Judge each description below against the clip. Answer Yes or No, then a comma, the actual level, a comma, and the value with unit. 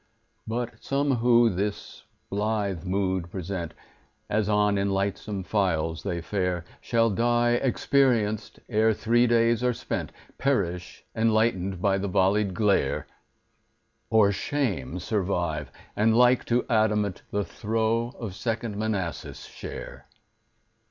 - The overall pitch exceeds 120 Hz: No, low, 105 Hz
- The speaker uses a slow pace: Yes, slow, 120 wpm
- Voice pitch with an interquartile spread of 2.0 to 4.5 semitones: Yes, average, 3.3 semitones